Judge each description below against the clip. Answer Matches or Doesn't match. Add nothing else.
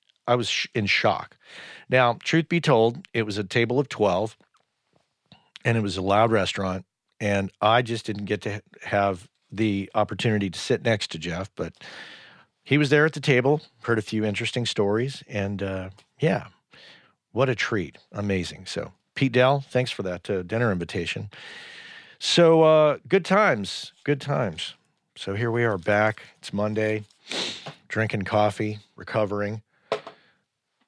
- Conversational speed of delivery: Matches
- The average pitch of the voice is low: Matches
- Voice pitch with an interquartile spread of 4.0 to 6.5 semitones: Matches